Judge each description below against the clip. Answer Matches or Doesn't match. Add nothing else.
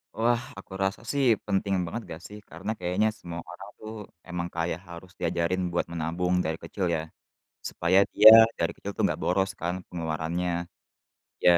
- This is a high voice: Doesn't match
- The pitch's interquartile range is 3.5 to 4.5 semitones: Doesn't match